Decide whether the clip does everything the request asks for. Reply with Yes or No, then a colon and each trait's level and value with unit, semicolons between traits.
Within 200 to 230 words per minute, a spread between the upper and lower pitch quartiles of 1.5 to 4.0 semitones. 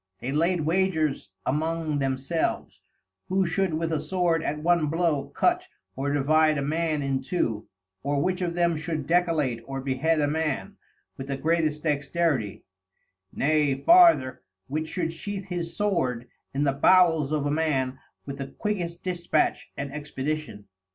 No: average, 150 wpm; average, 3.6 semitones